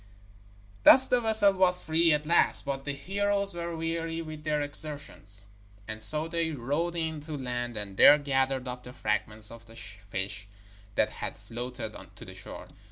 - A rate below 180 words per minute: Yes, average, 170 wpm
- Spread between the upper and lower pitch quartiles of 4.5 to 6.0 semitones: Yes, wide, 5.6 semitones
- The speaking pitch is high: No, medium, 145 Hz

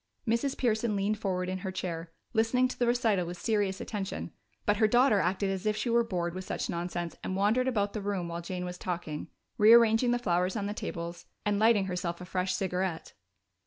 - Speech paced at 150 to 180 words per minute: No, fast, 205 wpm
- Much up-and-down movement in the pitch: No, average, 3.6 semitones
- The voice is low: No, high, 195 Hz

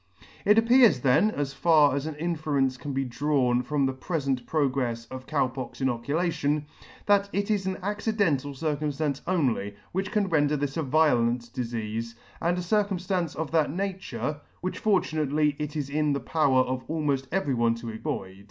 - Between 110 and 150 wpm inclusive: No, average, 170 wpm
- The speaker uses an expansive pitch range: No, average, 4.6 semitones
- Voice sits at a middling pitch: Yes, medium, 145 Hz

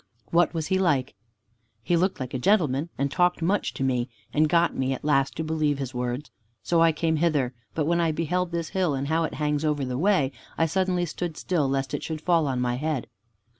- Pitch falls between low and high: Yes, medium, 155 Hz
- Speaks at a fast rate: Yes, fast, 225 wpm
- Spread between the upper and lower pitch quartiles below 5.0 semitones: Yes, average, 3.9 semitones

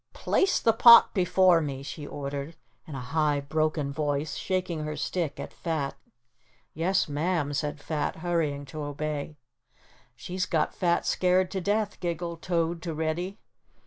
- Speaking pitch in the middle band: Yes, medium, 160 Hz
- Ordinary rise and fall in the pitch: Yes, average, 3.6 semitones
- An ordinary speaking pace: Yes, average, 145 wpm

